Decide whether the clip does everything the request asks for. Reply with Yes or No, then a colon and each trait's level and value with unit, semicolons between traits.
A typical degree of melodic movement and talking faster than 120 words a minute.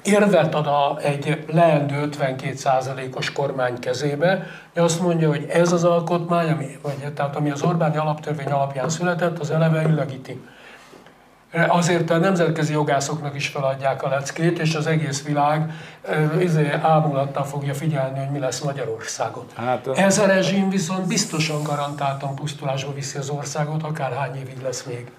Yes: average, 3.1 semitones; average, 145 wpm